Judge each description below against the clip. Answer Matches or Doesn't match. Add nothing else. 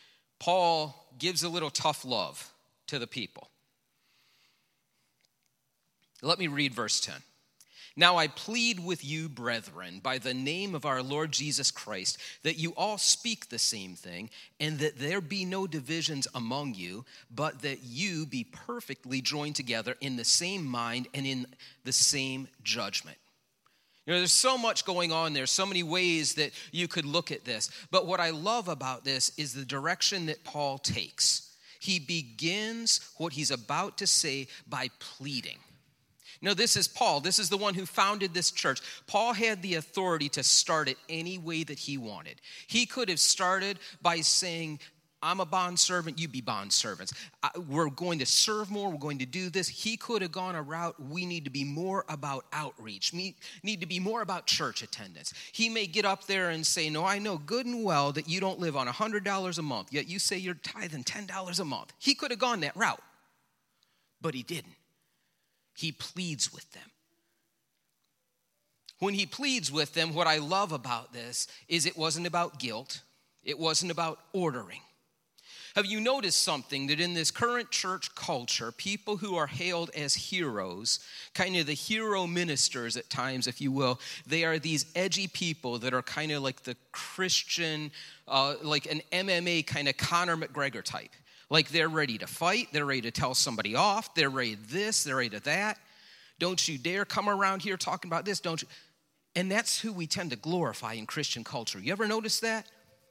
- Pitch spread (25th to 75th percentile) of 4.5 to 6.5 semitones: Matches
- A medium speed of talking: Matches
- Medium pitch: Matches